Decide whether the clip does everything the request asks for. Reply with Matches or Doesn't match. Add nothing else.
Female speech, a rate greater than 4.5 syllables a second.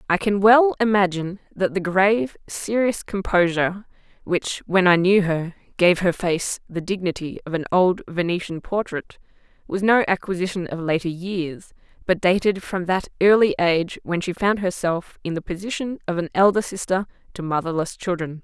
Matches